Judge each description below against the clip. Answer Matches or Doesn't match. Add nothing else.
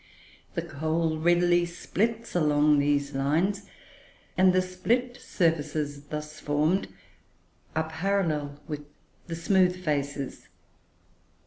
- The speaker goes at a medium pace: Doesn't match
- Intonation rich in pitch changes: Doesn't match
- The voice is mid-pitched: Matches